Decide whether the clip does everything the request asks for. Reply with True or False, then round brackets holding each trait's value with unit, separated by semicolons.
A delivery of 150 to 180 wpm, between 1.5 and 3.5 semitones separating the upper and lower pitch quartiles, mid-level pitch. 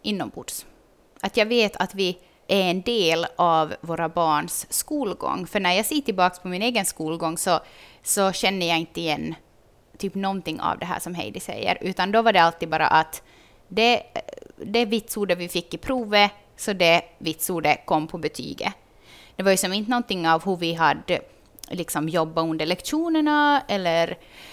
False (170 wpm; 4.2 semitones; 180 Hz)